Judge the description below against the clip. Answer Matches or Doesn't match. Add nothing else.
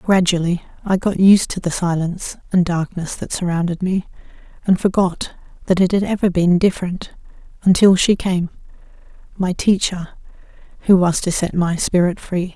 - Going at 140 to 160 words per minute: Matches